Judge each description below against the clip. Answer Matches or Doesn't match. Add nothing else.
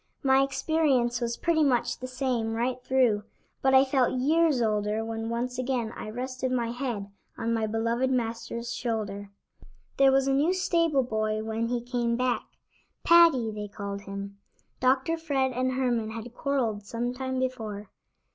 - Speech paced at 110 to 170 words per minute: Matches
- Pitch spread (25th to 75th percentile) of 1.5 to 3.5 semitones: Matches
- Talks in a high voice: Matches